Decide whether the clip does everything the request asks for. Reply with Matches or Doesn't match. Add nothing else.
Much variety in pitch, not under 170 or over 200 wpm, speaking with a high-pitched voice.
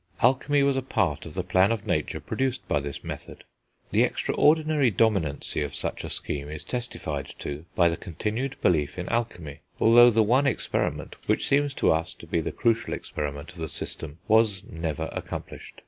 Doesn't match